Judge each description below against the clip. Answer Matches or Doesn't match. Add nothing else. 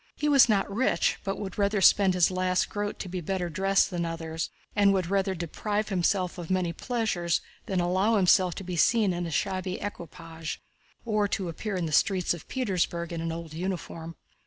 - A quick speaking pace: Doesn't match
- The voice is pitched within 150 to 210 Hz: Matches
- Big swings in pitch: Doesn't match